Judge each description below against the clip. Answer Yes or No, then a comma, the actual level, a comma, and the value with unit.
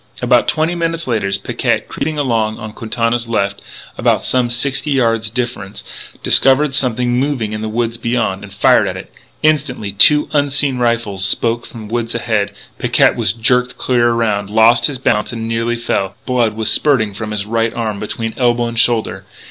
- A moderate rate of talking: Yes, average, 175 wpm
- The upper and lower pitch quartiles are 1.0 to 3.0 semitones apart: Yes, narrow, 2.5 semitones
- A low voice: Yes, low, 115 Hz